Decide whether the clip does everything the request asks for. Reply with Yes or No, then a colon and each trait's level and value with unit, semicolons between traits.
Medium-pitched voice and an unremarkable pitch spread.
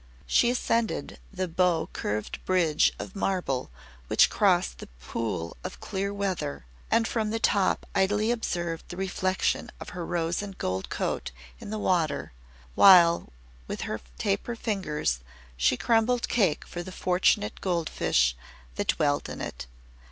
Yes: medium, 180 Hz; average, 5.0 semitones